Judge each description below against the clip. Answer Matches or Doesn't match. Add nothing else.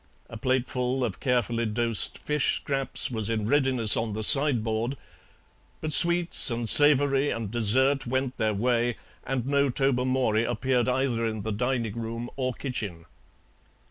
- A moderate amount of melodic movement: Matches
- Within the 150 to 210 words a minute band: Doesn't match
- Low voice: Matches